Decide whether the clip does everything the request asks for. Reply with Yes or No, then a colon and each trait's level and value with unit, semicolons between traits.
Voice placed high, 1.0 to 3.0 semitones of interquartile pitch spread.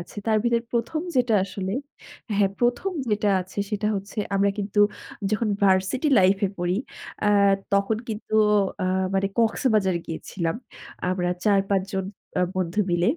Yes: high, 200 Hz; average, 2.7 semitones